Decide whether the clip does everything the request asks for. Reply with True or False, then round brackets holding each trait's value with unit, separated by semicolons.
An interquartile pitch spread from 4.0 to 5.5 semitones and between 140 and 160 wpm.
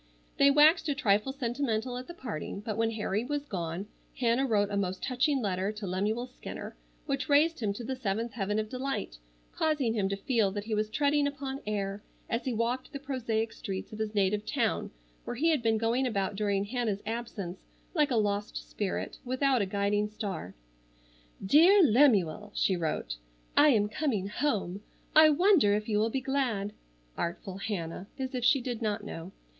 False (4.8 semitones; 185 wpm)